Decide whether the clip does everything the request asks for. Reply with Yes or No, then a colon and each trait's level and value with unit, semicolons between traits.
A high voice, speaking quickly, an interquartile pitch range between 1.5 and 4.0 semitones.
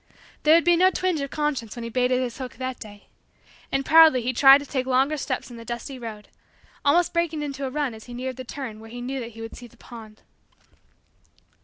Yes: very high, 255 Hz; fast, 230 wpm; average, 3.4 semitones